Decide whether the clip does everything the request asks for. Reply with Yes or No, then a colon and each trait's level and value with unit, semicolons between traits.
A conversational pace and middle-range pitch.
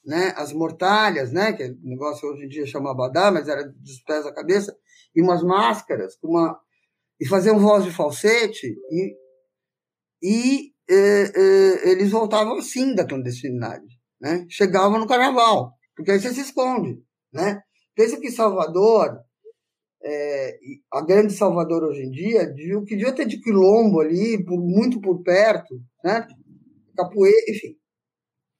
No: average, 160 wpm; high, 200 Hz